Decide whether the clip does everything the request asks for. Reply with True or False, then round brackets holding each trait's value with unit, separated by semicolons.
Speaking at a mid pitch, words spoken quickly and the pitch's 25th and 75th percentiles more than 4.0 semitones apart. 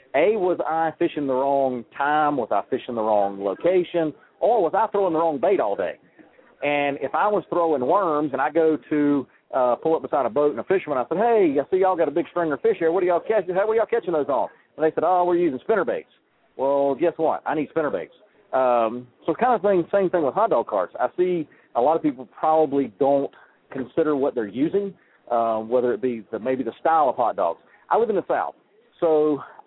True (155 Hz; 240 wpm; 4.8 semitones)